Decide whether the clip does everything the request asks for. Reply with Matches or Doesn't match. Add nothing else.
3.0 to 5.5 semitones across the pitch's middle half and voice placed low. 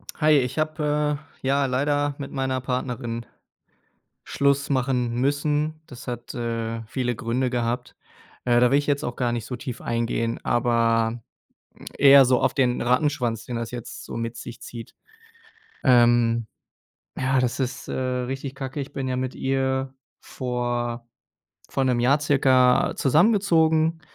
Doesn't match